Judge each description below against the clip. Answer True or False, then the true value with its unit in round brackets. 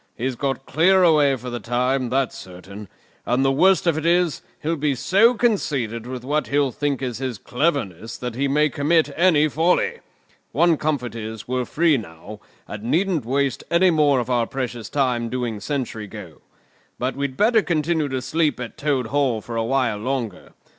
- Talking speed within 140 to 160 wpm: False (180 wpm)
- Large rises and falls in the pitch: False (4.3 semitones)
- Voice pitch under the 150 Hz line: True (135 Hz)